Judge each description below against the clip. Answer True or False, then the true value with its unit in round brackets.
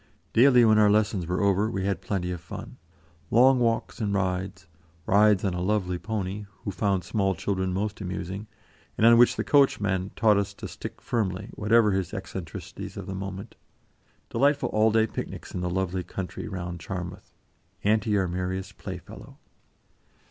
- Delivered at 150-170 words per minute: True (165 wpm)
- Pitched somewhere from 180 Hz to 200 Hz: False (100 Hz)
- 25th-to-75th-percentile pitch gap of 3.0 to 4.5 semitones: False (2.6 semitones)